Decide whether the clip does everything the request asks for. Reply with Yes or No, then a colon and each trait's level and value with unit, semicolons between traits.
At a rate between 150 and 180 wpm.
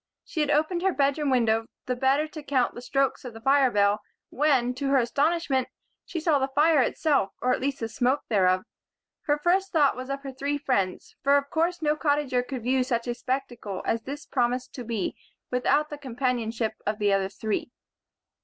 No: average, 200 wpm